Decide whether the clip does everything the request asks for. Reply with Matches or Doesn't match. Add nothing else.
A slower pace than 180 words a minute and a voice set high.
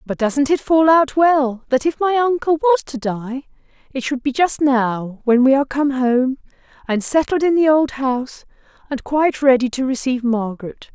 Doesn't match